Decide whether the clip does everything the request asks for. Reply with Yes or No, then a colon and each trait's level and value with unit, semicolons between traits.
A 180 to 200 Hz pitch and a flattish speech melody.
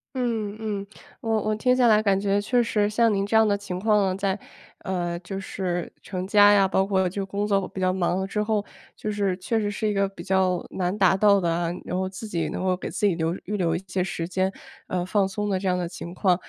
Yes: high, 195 Hz; narrow, 2.2 semitones